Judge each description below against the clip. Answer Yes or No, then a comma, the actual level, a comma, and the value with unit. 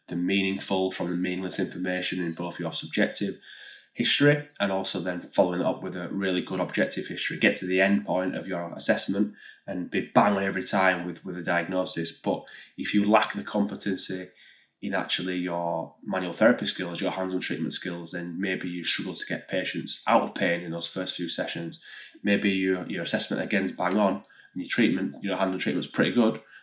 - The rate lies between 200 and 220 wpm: Yes, fast, 205 wpm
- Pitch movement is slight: Yes, narrow, 1.6 semitones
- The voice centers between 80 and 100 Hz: Yes, very low, 90 Hz